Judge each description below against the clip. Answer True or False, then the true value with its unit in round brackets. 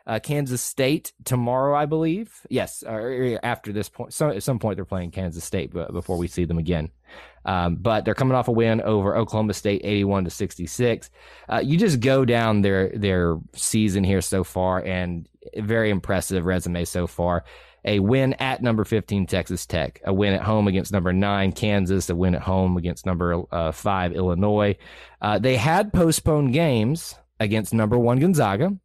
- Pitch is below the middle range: True (100 Hz)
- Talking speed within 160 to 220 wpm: True (180 wpm)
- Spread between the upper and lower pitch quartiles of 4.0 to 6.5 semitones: True (4.6 semitones)